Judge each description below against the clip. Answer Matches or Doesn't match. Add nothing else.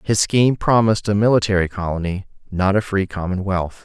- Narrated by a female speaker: Doesn't match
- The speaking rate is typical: Matches